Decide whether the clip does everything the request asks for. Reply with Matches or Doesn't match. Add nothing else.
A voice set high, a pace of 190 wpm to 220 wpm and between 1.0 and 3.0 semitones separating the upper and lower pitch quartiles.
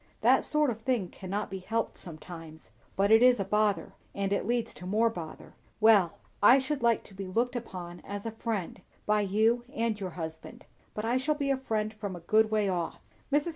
Doesn't match